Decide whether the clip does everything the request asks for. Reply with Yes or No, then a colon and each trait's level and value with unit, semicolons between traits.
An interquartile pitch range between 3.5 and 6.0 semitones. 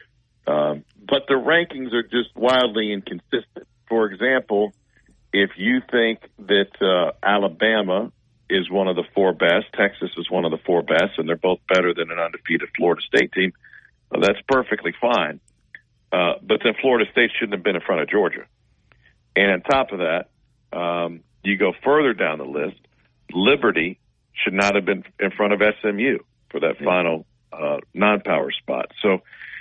Yes: average, 4.6 semitones